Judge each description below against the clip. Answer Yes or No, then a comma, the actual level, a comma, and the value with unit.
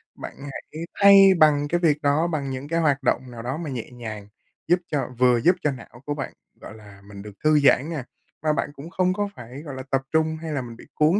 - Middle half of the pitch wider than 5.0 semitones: No, average, 4.1 semitones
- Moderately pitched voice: Yes, medium, 145 Hz